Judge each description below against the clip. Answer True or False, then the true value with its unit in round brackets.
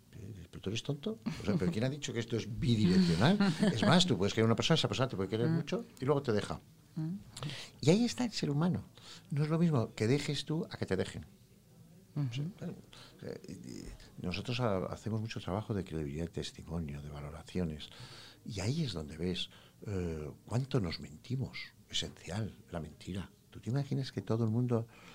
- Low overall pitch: True (115 Hz)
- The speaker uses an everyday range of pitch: False (8.0 semitones)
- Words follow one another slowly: False (180 wpm)